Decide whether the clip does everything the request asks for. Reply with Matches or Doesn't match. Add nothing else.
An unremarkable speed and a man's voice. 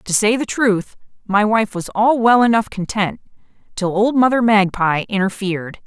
Doesn't match